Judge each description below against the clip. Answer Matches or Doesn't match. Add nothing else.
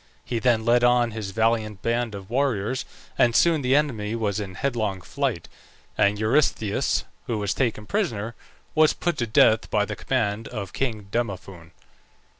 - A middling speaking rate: Matches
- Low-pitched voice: Matches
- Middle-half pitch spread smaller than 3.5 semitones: Matches